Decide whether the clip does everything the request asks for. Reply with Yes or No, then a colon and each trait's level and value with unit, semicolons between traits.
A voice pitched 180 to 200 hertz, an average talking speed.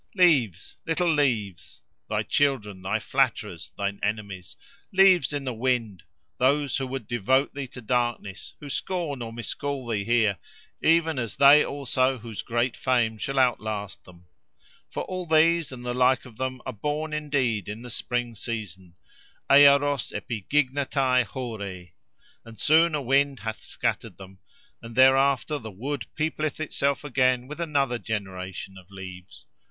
No: low, 125 Hz; average, 145 wpm